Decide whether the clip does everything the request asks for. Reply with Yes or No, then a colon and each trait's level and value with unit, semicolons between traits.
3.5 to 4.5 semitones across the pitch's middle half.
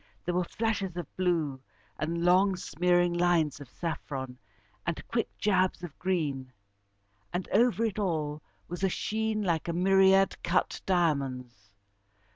Yes: average, 3.8 semitones